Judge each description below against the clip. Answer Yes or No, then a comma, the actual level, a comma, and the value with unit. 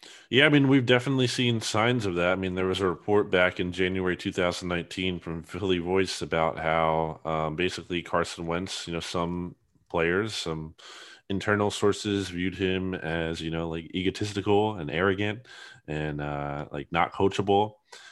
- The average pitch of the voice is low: Yes, very low, 90 Hz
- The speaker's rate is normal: Yes, average, 160 wpm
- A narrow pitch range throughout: No, average, 3.6 semitones